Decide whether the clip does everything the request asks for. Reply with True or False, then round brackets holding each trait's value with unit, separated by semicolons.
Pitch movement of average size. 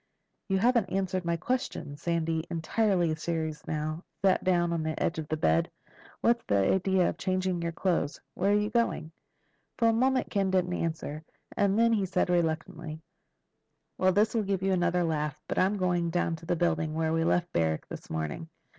True (3.2 semitones)